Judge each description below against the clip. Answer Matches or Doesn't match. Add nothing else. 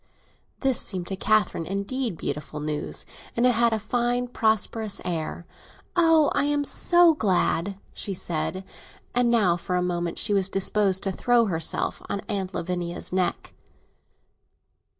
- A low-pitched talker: Doesn't match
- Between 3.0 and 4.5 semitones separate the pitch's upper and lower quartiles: Doesn't match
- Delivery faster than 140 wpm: Doesn't match